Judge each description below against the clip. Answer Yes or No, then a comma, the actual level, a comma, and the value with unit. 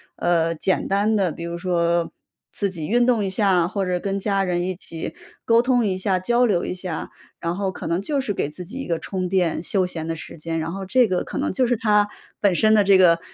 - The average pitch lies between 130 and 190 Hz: Yes, medium, 185 Hz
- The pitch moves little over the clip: No, average, 3.3 semitones